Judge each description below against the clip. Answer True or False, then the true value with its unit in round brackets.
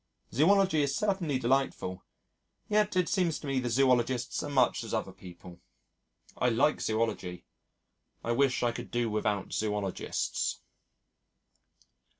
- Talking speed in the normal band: False (130 wpm)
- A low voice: True (125 Hz)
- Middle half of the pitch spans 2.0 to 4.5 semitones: False (5.3 semitones)